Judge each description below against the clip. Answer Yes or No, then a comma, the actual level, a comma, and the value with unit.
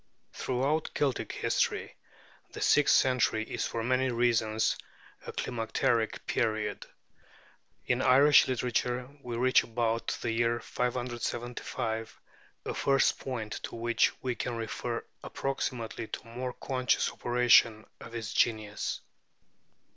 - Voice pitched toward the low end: Yes, low, 120 Hz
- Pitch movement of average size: No, narrow, 2.0 semitones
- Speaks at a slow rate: Yes, slow, 115 wpm